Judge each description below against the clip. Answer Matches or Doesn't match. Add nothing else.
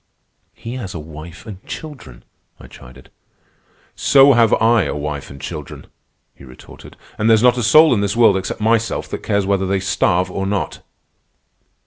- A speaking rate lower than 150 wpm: Doesn't match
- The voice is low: Matches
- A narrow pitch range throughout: Doesn't match